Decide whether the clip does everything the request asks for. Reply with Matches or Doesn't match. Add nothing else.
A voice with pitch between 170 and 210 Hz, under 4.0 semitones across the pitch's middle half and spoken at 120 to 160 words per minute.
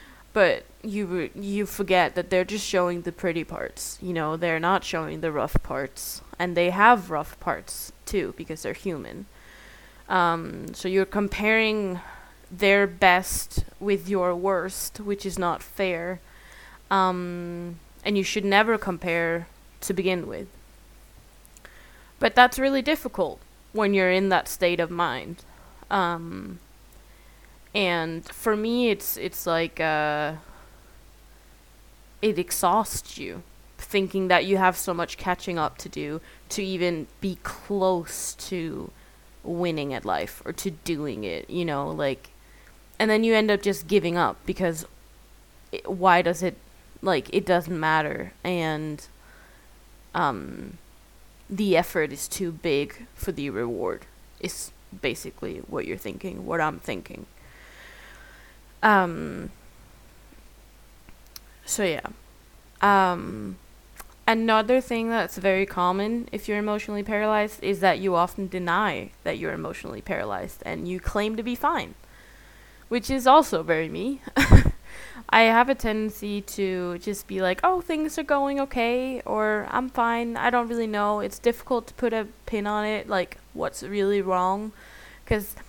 Matches